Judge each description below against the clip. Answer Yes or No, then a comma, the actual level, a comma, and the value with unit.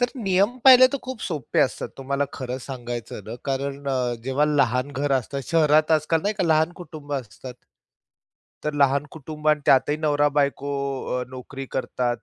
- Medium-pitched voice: Yes, medium, 145 Hz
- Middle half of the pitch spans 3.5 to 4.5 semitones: No, average, 3.0 semitones